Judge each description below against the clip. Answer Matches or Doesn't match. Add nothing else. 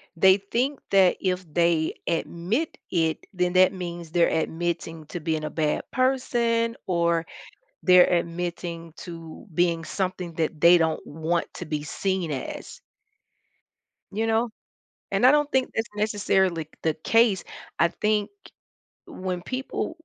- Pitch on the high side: Doesn't match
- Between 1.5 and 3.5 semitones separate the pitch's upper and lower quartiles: Doesn't match